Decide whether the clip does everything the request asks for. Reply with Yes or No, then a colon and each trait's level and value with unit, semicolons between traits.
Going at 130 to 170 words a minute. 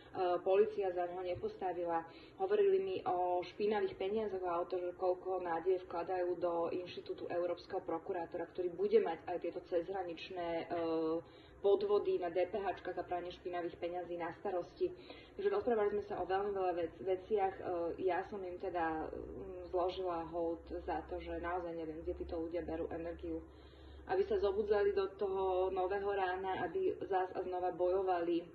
Yes: average, 150 wpm